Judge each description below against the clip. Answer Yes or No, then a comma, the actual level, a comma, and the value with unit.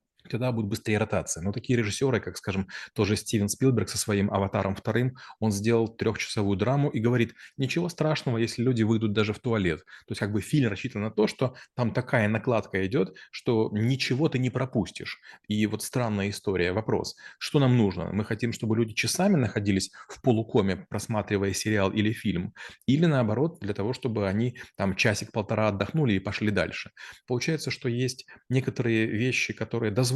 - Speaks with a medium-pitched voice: No, low, 110 Hz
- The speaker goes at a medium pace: No, fast, 175 wpm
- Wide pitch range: No, average, 3.4 semitones